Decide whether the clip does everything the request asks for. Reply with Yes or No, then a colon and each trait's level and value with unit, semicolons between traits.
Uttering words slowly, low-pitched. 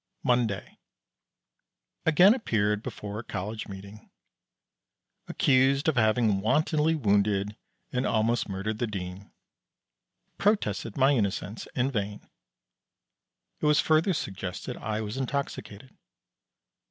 Yes: slow, 105 wpm; low, 110 Hz